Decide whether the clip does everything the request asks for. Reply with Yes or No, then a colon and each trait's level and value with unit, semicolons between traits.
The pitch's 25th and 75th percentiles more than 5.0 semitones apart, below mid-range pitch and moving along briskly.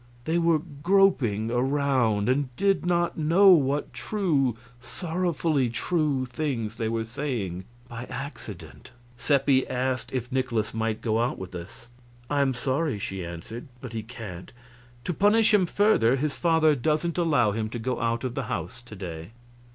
No: wide, 5.6 semitones; low, 130 Hz; average, 160 wpm